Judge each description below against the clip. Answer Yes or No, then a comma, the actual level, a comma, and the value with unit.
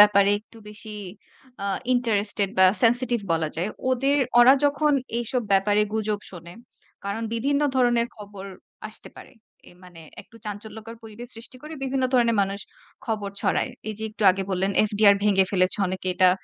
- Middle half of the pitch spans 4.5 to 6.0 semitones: No, average, 3.3 semitones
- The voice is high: Yes, high, 215 Hz